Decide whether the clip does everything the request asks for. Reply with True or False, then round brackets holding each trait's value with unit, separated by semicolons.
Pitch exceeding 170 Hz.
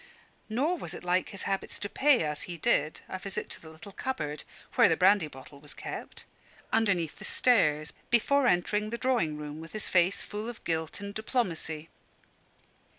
True (185 Hz)